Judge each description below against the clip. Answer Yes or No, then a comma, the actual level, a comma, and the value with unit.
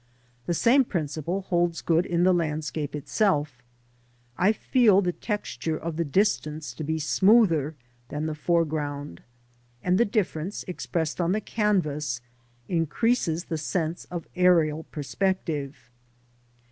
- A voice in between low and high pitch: Yes, medium, 165 Hz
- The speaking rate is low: Yes, slow, 125 wpm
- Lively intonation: No, average, 3.7 semitones